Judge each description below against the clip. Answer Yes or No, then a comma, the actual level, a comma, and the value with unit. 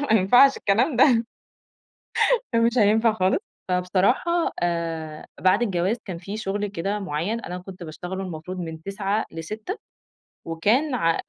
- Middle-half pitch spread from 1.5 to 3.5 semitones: No, average, 4.5 semitones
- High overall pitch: Yes, high, 195 Hz